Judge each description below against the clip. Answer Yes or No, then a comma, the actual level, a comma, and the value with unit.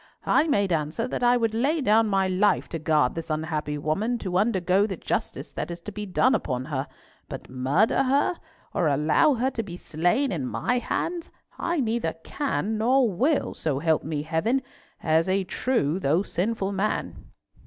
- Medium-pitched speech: No, high, 195 Hz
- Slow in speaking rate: No, average, 180 wpm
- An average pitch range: No, wide, 7.0 semitones